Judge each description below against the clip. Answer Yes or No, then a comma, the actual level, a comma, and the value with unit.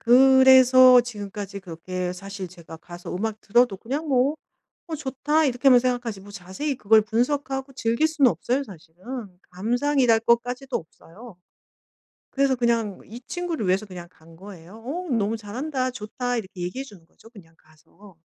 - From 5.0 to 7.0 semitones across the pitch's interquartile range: Yes, wide, 5.4 semitones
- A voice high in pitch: Yes, high, 230 Hz